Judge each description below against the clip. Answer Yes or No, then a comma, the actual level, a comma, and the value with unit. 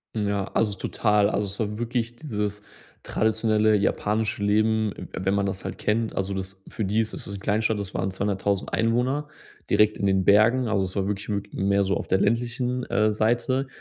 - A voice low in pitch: Yes, low, 105 Hz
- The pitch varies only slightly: Yes, narrow, 2.0 semitones